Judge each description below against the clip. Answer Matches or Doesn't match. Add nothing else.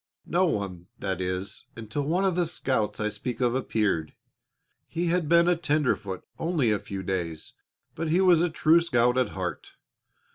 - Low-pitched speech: Matches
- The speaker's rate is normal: Matches